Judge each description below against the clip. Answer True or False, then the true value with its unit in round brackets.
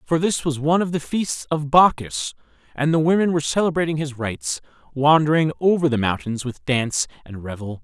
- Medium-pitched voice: True (145 Hz)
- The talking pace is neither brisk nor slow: True (185 wpm)